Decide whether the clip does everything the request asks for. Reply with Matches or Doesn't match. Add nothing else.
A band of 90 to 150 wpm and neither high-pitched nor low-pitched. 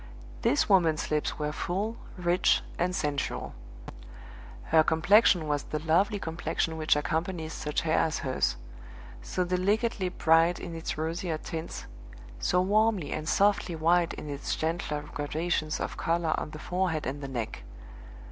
Matches